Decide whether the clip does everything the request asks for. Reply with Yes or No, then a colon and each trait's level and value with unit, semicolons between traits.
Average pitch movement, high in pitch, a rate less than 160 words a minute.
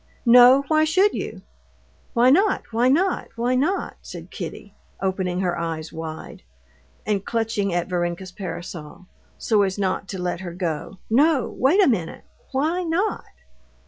No: wide, 7.6 semitones; high, 210 Hz; average, 145 wpm